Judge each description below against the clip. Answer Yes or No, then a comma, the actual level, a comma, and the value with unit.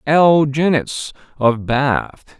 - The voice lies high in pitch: No, medium, 140 Hz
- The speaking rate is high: No, slow, 100 wpm